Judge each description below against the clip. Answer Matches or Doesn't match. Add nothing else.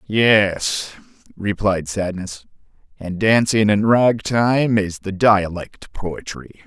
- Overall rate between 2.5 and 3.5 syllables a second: Matches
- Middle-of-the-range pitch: Doesn't match